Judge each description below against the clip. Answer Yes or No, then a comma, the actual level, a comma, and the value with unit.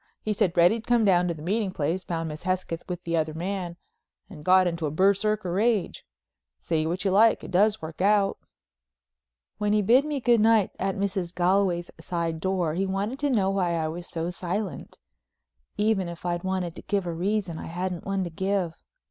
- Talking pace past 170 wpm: Yes, average, 200 wpm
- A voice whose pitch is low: No, medium, 185 Hz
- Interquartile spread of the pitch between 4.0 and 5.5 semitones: No, average, 2.9 semitones